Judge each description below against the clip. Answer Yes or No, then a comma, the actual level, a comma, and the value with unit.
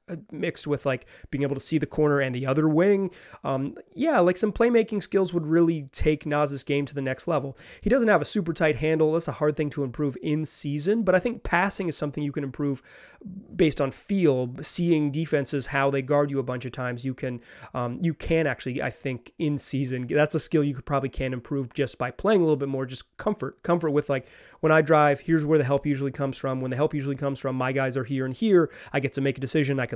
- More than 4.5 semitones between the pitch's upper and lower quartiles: No, average, 3.0 semitones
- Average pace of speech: No, fast, 250 wpm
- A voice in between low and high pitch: Yes, medium, 145 Hz